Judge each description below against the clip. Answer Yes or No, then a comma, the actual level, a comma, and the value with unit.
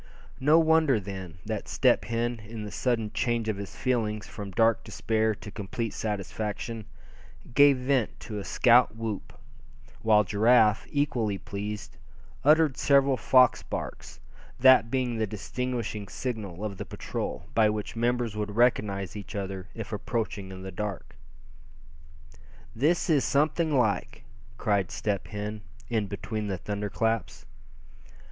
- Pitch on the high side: No, low, 110 Hz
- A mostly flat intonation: No, average, 3.2 semitones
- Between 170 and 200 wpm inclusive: No, average, 140 wpm